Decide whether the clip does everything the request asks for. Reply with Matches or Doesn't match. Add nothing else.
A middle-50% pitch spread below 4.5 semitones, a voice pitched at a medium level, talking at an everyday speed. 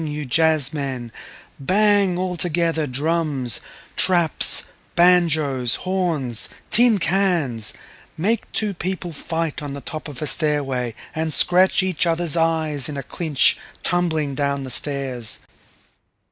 Doesn't match